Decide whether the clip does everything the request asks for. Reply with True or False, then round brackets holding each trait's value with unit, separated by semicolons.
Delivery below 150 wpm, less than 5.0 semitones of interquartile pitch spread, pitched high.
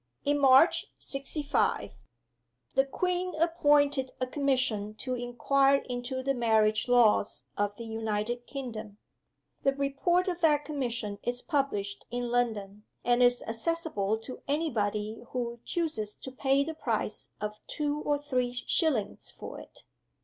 True (140 wpm; 4.5 semitones; 255 Hz)